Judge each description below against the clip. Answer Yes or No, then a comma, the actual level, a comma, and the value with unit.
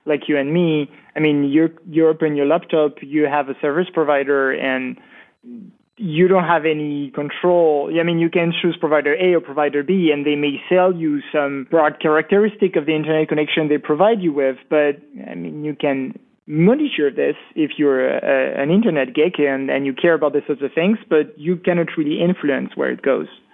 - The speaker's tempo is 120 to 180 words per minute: No, average, 200 wpm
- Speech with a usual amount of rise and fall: Yes, average, 3.0 semitones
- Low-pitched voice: No, medium, 155 Hz